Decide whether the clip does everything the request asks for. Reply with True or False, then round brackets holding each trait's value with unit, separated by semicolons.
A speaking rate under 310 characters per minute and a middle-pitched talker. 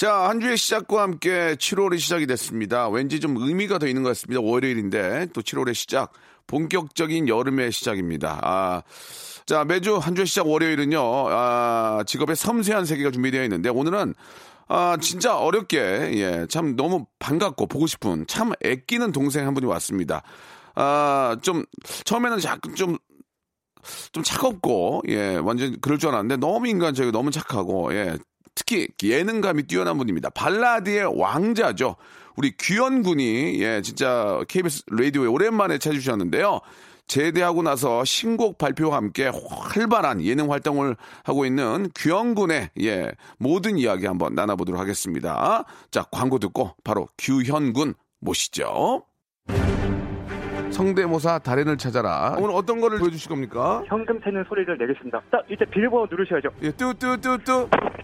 False (320 characters per minute; 150 Hz)